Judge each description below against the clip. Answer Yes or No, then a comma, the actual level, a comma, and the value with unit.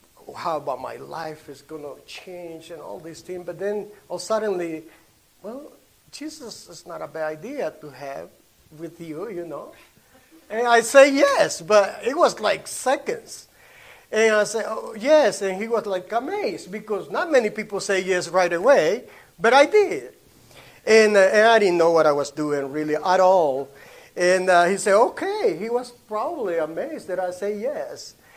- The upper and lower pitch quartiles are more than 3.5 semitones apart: Yes, wide, 5.5 semitones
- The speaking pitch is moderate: No, high, 195 Hz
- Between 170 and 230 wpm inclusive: Yes, average, 180 wpm